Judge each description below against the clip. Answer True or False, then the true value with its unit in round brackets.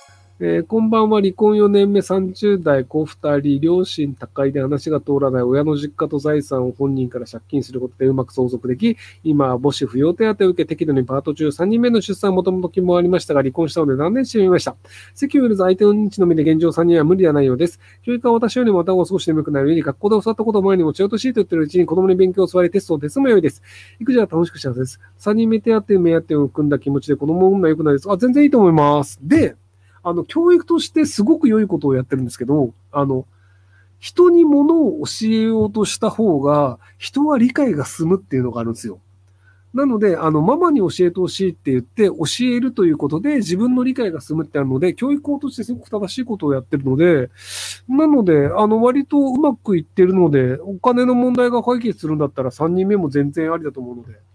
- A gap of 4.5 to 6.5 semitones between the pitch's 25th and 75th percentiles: False (7.5 semitones)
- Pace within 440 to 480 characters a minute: True (445 characters per minute)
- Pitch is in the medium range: True (170 Hz)